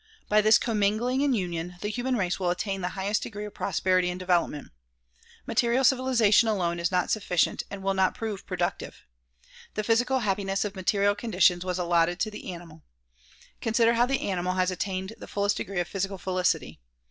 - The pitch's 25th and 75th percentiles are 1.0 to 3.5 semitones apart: Yes, average, 3.1 semitones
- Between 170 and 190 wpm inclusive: Yes, average, 180 wpm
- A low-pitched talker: No, high, 195 Hz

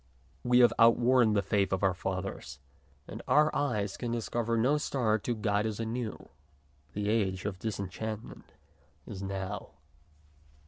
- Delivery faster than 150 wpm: No, average, 145 wpm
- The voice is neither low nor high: No, low, 110 Hz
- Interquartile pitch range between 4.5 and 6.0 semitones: No, average, 3.3 semitones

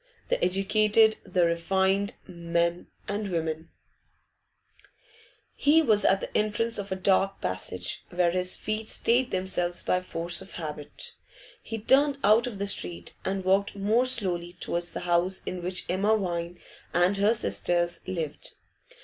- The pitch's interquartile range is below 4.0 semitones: Yes, average, 3.3 semitones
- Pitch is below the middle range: No, high, 190 Hz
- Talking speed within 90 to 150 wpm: Yes, average, 145 wpm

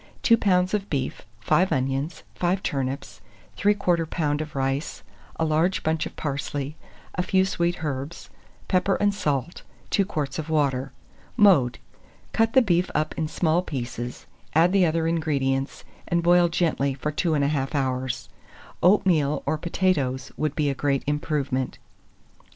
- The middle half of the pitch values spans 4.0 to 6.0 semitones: Yes, average, 4.4 semitones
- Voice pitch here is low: No, medium, 155 Hz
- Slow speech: No, average, 145 wpm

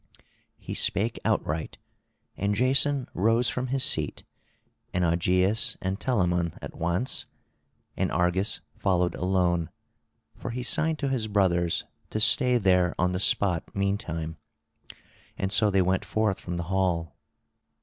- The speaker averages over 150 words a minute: No, slow, 135 wpm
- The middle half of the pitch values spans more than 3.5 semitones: Yes, average, 4.3 semitones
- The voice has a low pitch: Yes, very low, 95 Hz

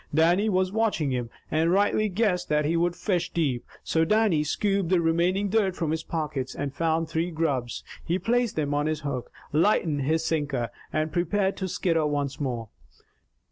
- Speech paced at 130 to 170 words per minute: No, average, 180 wpm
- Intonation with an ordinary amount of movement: Yes, average, 4.0 semitones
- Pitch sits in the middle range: Yes, medium, 165 Hz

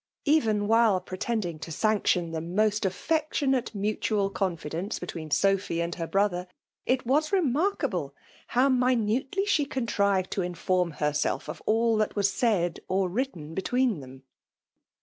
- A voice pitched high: Yes, high, 205 Hz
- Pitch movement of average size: No, wide, 5.7 semitones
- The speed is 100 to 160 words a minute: Yes, average, 150 wpm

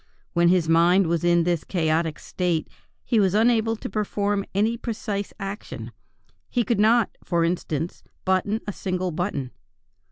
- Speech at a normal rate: Yes, average, 150 wpm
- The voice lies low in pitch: No, medium, 185 Hz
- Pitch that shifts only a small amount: No, average, 3.7 semitones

